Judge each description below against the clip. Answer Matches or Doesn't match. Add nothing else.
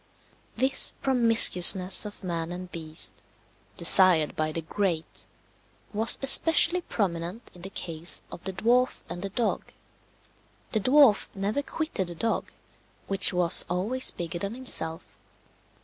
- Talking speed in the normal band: Doesn't match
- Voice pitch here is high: Matches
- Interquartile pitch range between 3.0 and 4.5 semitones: Doesn't match